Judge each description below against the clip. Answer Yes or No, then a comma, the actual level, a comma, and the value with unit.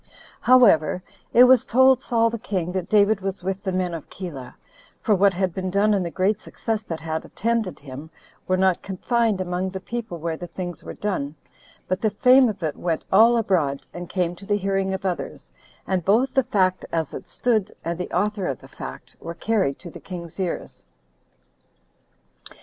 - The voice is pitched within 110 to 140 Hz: No, high, 190 Hz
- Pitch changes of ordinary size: Yes, average, 3.4 semitones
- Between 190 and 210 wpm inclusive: Yes, average, 195 wpm